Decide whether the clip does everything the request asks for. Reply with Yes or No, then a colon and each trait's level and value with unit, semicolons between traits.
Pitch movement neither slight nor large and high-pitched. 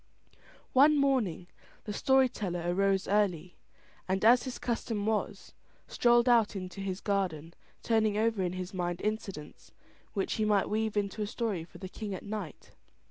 Yes: average, 3.3 semitones; high, 205 Hz